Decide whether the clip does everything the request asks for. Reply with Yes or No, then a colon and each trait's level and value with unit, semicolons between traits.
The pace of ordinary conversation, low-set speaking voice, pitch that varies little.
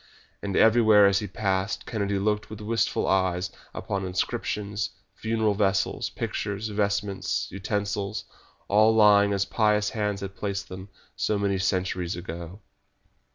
No: slow, 130 wpm; low, 100 Hz; narrow, 1.6 semitones